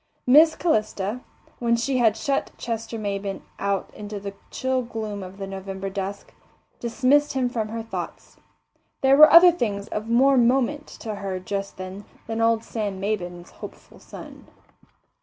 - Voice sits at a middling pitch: No, high, 220 Hz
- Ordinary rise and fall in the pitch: Yes, average, 4.1 semitones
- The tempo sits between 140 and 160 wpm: Yes, average, 155 wpm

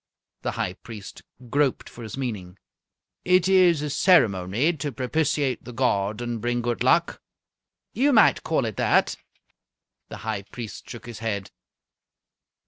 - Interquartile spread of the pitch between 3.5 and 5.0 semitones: No, wide, 5.5 semitones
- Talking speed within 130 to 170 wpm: Yes, average, 140 wpm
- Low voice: Yes, low, 120 Hz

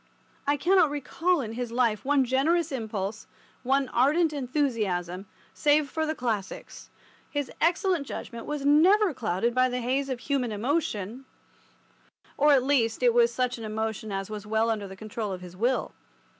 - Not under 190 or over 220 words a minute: No, average, 160 wpm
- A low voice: No, very high, 250 Hz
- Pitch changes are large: No, average, 4.8 semitones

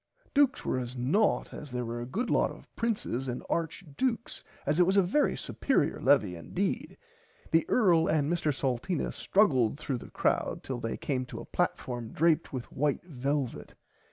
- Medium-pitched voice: Yes, medium, 145 Hz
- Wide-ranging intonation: Yes, wide, 6.1 semitones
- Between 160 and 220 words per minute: Yes, average, 180 wpm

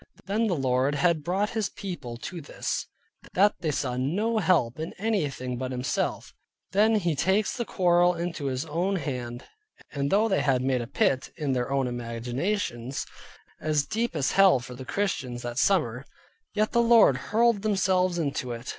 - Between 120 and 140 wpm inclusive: No, average, 175 wpm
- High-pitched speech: No, medium, 155 Hz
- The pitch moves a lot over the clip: Yes, wide, 7.4 semitones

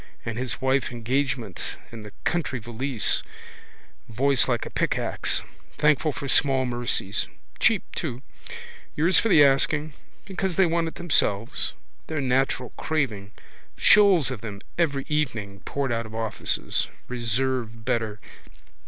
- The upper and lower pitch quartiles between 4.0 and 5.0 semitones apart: Yes, average, 4.5 semitones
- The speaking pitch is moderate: No, low, 130 Hz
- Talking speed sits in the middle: No, slow, 130 wpm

